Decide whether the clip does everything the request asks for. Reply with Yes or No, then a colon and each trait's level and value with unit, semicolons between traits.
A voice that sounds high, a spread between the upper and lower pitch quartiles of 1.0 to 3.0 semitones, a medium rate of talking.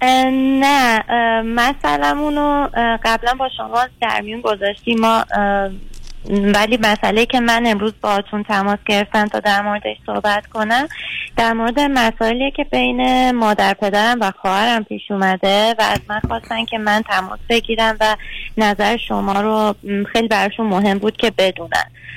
Yes: high, 220 Hz; narrow, 2.4 semitones; average, 145 wpm